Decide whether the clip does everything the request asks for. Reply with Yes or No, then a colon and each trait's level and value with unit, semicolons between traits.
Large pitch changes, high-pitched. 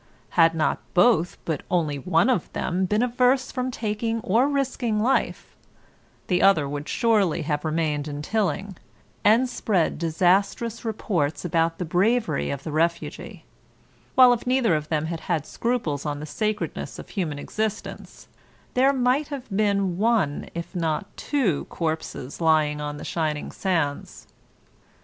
No: wide, 6.5 semitones; medium, 180 Hz